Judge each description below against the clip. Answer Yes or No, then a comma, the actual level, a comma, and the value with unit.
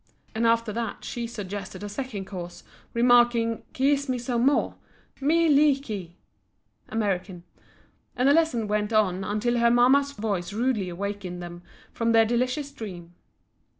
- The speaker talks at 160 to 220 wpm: No, average, 150 wpm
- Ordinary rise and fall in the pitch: Yes, average, 4.0 semitones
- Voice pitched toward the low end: No, high, 230 Hz